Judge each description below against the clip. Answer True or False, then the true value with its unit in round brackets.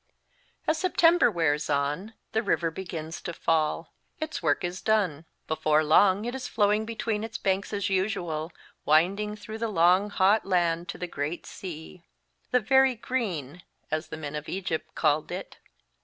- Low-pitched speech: False (185 Hz)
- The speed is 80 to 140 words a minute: False (165 wpm)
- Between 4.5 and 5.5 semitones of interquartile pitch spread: True (5.2 semitones)